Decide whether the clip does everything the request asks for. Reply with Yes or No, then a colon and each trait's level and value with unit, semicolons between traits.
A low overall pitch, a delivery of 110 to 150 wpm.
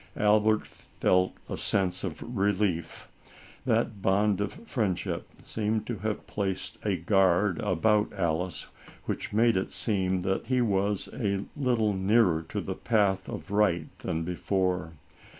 Yes: low, 100 Hz; slow, 135 wpm